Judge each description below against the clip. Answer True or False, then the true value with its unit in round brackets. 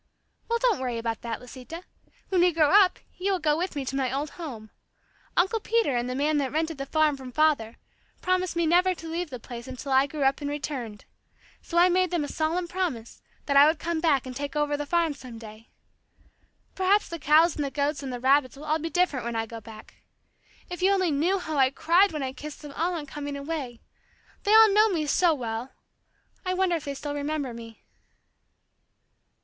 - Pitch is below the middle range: False (295 Hz)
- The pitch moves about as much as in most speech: True (4.7 semitones)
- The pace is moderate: False (220 wpm)